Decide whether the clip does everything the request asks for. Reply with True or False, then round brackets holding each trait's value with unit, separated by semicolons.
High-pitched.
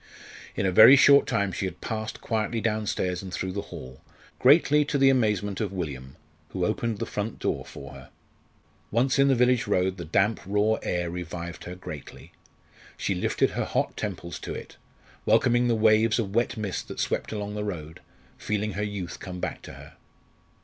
False (105 Hz)